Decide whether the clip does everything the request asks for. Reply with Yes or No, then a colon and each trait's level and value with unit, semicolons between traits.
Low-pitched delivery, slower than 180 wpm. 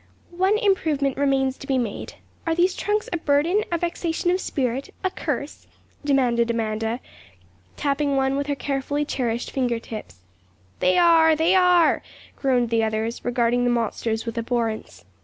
No: very high, 270 Hz; average, 155 wpm